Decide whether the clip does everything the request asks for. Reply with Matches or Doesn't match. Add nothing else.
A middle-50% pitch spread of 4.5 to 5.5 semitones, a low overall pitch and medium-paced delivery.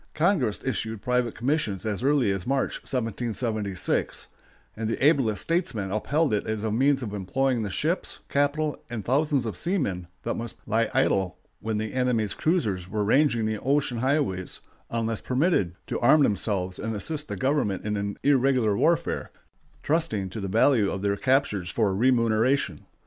Matches